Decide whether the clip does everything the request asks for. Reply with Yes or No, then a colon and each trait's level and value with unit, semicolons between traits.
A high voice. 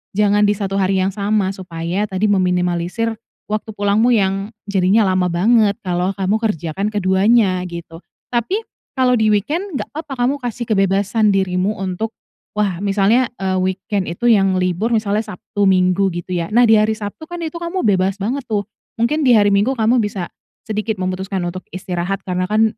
Yes: high, 200 Hz